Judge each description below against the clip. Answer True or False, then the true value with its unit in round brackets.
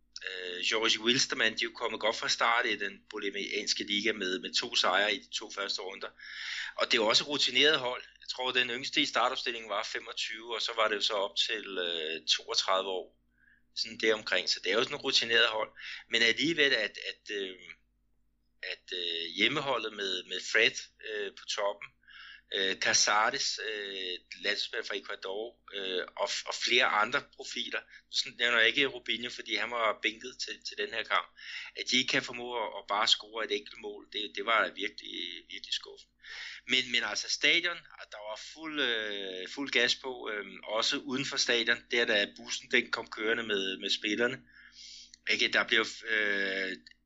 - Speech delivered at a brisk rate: False (180 wpm)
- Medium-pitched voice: False (130 Hz)